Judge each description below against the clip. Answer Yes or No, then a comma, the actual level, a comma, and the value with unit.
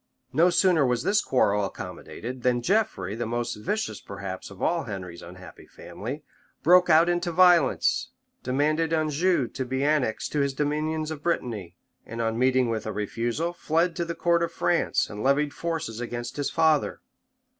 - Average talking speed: Yes, average, 165 wpm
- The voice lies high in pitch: No, medium, 140 Hz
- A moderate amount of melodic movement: No, wide, 6.1 semitones